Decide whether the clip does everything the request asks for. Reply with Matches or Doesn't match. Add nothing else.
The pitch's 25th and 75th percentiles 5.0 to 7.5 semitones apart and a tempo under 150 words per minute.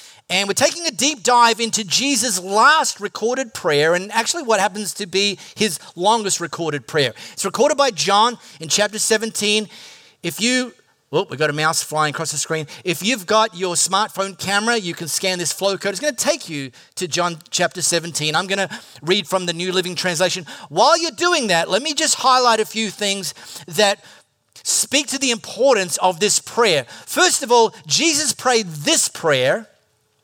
Doesn't match